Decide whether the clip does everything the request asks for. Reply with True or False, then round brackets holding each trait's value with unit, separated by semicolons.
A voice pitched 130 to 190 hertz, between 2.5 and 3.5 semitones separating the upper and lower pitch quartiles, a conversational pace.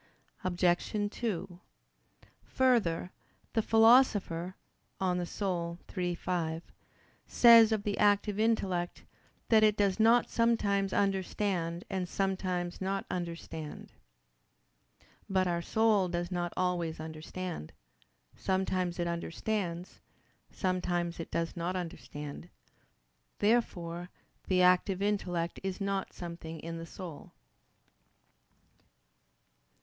False (185 Hz; 2.9 semitones; 100 wpm)